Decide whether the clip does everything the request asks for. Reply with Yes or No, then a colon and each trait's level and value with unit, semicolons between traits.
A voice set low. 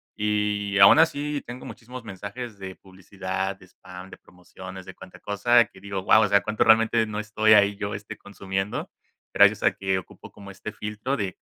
Yes: low, 100 Hz